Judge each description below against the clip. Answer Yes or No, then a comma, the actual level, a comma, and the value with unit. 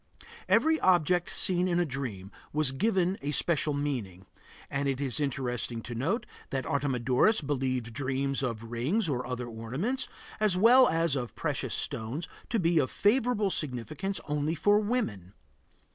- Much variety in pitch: Yes, wide, 6.5 semitones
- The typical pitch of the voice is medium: Yes, medium, 145 Hz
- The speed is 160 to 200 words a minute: No, average, 150 wpm